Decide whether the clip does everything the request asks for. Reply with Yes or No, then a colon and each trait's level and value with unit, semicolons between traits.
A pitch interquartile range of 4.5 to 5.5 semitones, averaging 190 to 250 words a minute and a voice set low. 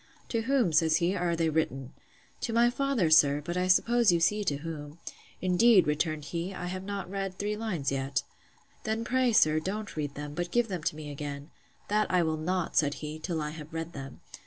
No: average, 5.1 semitones; fast, 205 wpm; medium, 170 Hz